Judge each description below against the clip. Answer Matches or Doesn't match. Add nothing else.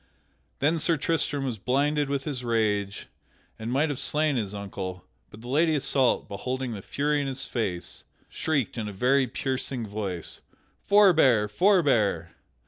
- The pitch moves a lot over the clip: Matches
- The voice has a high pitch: Doesn't match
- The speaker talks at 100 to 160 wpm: Matches